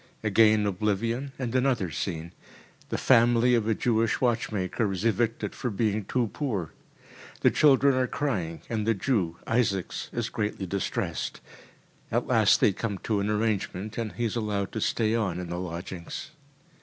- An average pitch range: Yes, average, 3.4 semitones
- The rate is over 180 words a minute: No, average, 160 wpm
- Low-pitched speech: Yes, low, 110 Hz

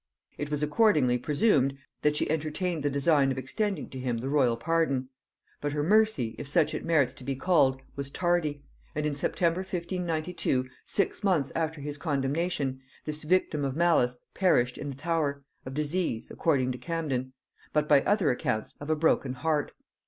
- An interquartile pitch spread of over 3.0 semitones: Yes, average, 3.7 semitones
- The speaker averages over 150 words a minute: Yes, average, 175 wpm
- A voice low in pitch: No, medium, 150 Hz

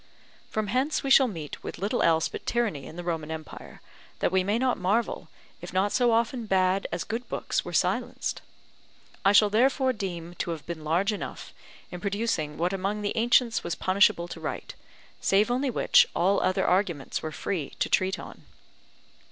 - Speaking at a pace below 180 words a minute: No, average, 185 wpm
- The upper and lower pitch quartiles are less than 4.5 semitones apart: No, average, 4.8 semitones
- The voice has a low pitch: No, high, 195 Hz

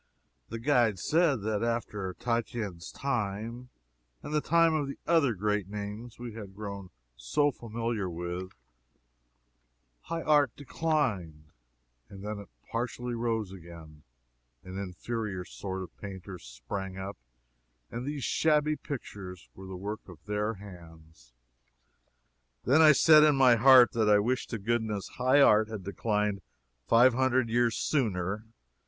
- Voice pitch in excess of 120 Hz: No, low, 110 Hz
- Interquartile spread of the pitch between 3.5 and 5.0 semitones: Yes, average, 4.7 semitones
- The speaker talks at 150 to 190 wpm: No, slow, 135 wpm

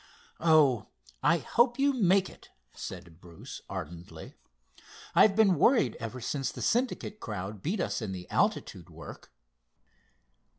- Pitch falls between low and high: Yes, medium, 145 Hz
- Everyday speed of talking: No, slow, 125 wpm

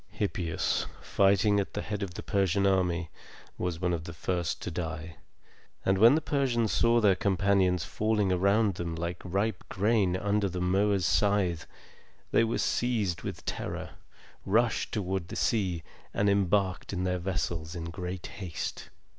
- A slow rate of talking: No, average, 155 wpm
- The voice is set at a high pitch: No, very low, 95 Hz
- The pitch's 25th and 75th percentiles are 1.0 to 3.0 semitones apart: Yes, average, 2.7 semitones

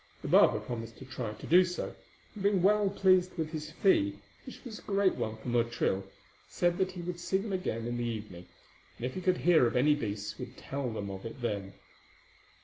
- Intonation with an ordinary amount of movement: No, wide, 8.4 semitones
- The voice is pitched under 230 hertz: Yes, medium, 140 Hz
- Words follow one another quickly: Yes, fast, 220 wpm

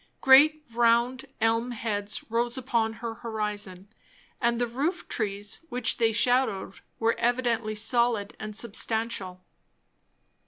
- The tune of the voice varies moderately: No, narrow, 2.2 semitones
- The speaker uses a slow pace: Yes, slow, 115 wpm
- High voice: Yes, high, 230 Hz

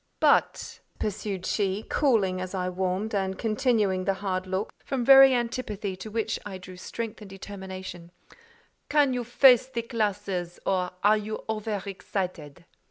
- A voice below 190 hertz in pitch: No, high, 205 Hz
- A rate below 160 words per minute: Yes, average, 150 wpm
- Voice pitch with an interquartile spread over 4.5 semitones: No, average, 3.2 semitones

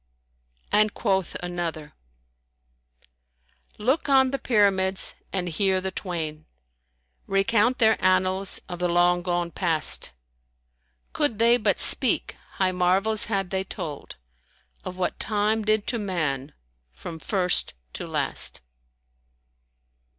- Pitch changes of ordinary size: Yes, average, 3.3 semitones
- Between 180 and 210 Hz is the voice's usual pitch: Yes, high, 190 Hz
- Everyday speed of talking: No, slow, 120 wpm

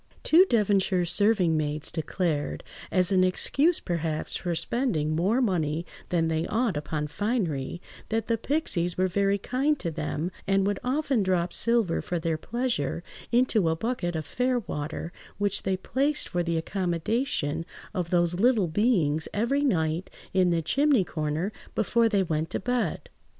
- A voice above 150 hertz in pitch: Yes, medium, 185 Hz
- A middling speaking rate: Yes, average, 150 wpm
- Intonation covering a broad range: Yes, wide, 6.0 semitones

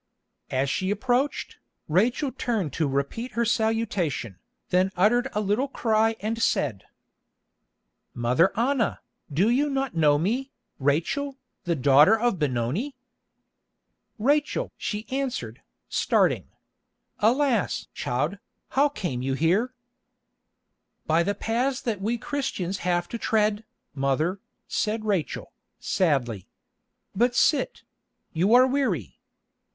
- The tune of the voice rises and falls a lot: Yes, wide, 7.4 semitones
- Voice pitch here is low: No, high, 210 Hz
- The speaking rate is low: Yes, slow, 115 wpm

